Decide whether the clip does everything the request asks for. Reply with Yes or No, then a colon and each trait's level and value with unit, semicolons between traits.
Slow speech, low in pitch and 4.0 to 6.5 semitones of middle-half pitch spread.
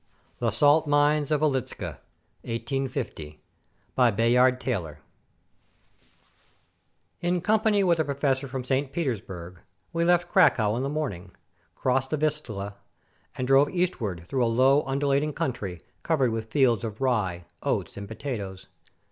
Yes: slow, 130 wpm; low, 130 Hz; average, 4.8 semitones